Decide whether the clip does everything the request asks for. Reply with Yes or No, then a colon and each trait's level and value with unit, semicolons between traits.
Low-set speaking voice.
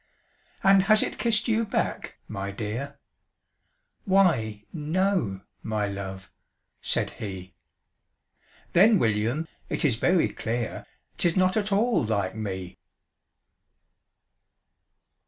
Yes: low, 125 Hz